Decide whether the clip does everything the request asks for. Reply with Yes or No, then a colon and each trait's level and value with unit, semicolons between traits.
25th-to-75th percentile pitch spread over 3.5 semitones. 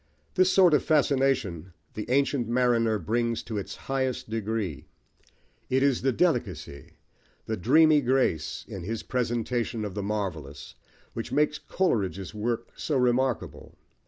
Yes: average, 4.4 semitones